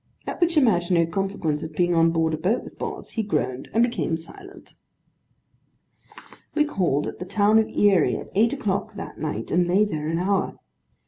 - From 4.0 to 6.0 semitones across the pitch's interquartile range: Yes, average, 4.8 semitones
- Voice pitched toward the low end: No, medium, 185 Hz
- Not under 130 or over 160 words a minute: No, average, 185 wpm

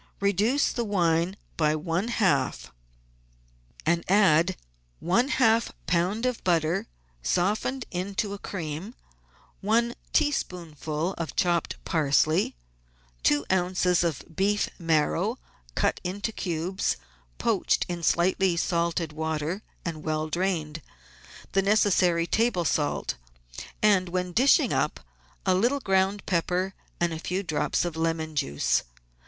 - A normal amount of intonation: Yes, average, 3.6 semitones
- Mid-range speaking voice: Yes, medium, 180 Hz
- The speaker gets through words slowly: Yes, slow, 115 wpm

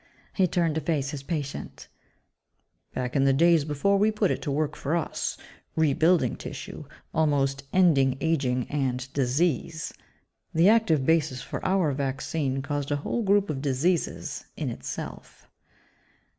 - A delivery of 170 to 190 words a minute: No, average, 145 wpm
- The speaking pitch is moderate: Yes, medium, 150 Hz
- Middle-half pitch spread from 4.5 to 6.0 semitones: No, average, 3.7 semitones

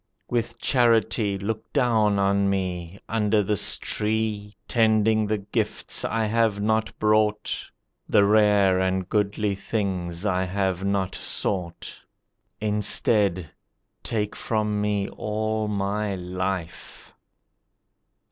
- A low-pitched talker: Yes, low, 105 Hz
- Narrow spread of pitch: Yes, narrow, 1.9 semitones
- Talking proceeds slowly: Yes, slow, 105 wpm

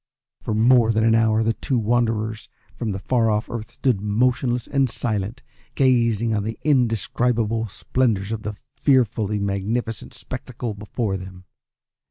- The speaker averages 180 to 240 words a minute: No, average, 145 wpm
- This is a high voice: No, low, 115 Hz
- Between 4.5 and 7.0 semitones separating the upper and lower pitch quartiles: No, narrow, 2.4 semitones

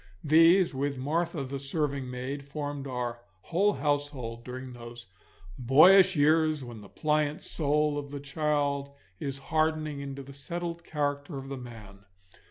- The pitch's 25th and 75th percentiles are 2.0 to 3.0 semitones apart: Yes, narrow, 2.6 semitones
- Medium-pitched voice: Yes, medium, 145 Hz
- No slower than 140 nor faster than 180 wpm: Yes, average, 145 wpm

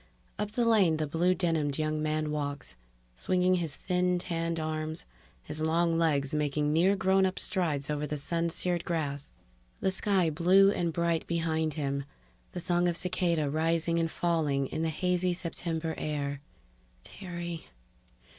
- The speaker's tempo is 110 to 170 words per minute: Yes, average, 155 wpm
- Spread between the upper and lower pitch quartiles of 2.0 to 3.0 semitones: Yes, narrow, 2.6 semitones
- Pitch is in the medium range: Yes, medium, 165 Hz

